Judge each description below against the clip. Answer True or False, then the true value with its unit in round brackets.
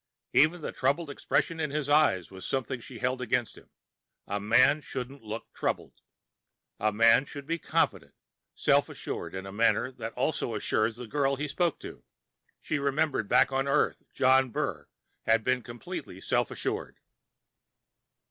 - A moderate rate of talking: True (160 wpm)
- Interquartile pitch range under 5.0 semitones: True (3.9 semitones)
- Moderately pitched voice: False (130 Hz)